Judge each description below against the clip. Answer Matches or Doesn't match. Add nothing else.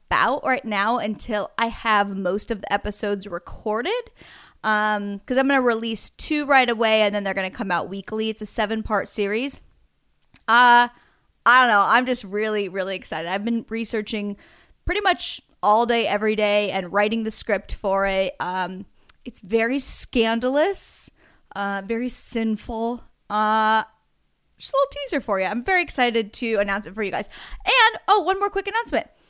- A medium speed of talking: Matches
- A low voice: Doesn't match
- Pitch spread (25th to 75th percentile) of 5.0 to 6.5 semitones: Doesn't match